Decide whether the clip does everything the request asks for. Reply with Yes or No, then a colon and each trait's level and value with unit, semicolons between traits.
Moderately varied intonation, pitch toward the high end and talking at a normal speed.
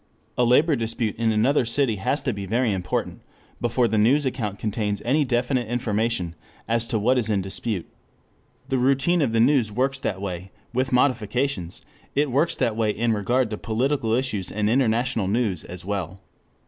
No: average, 3.6 semitones; low, 115 Hz; average, 175 wpm